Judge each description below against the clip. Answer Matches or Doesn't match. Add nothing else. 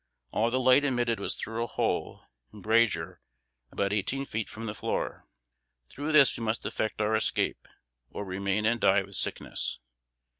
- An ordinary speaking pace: Matches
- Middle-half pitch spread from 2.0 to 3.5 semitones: Matches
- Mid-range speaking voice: Doesn't match